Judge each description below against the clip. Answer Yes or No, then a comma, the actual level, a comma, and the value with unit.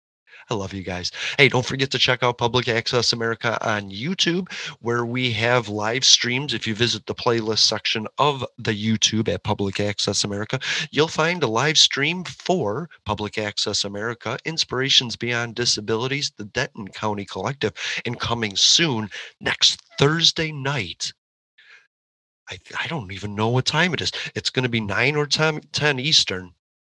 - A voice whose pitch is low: Yes, low, 120 Hz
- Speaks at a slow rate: No, average, 165 wpm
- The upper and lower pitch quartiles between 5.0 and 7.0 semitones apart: No, average, 4.3 semitones